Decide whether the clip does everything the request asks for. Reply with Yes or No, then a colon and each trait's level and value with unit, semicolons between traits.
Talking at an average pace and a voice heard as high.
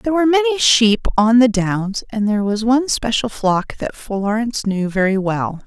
Yes: average, 190 wpm; high, 225 Hz